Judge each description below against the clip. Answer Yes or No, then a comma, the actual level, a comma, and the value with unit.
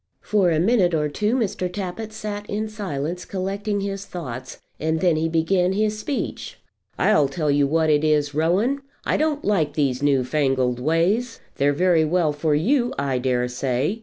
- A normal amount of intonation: No, wide, 5.9 semitones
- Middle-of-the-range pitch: Yes, medium, 165 Hz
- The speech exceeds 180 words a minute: No, average, 175 wpm